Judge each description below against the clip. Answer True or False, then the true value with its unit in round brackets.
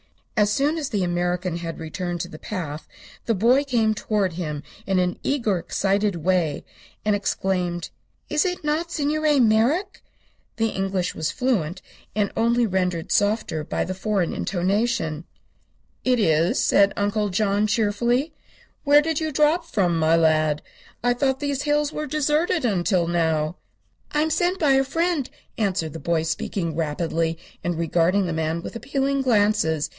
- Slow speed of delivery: False (155 wpm)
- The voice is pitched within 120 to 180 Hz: False (205 Hz)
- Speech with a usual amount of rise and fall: False (7.6 semitones)